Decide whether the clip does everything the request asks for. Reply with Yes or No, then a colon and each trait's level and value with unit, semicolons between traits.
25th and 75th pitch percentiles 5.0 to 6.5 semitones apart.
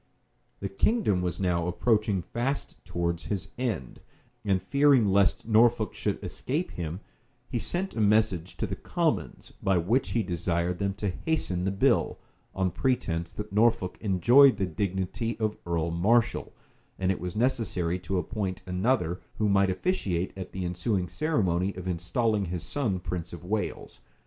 No: average, 4.4 semitones